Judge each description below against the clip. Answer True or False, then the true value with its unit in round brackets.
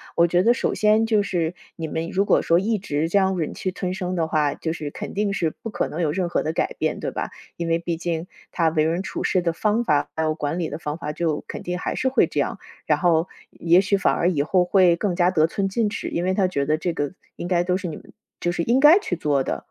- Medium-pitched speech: True (175 Hz)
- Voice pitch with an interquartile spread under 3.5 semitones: True (3.0 semitones)